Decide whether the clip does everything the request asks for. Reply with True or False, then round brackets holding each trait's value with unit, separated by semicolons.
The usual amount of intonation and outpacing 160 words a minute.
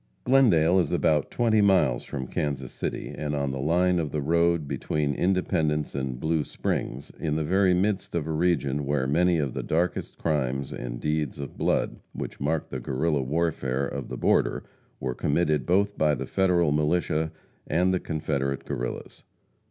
True (3.8 semitones; 170 wpm)